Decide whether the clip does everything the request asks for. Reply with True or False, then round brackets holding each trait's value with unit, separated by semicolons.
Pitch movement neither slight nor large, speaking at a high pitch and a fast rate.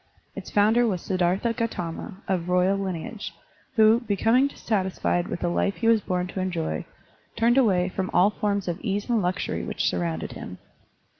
False (3.7 semitones; 195 Hz; 170 wpm)